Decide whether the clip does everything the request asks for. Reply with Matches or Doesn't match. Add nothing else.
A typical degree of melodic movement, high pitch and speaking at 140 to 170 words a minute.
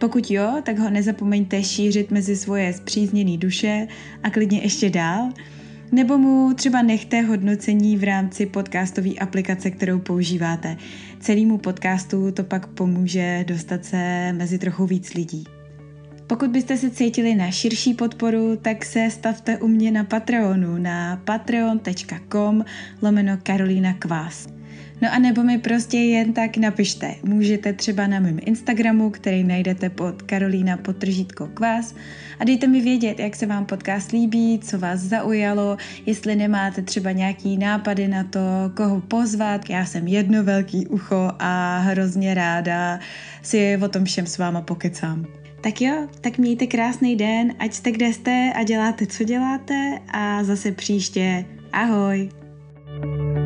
Matches